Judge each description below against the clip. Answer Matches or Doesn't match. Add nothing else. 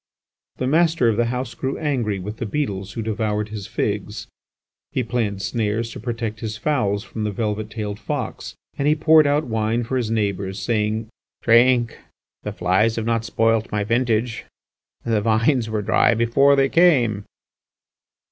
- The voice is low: Matches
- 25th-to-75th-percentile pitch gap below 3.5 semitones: Matches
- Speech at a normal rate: Matches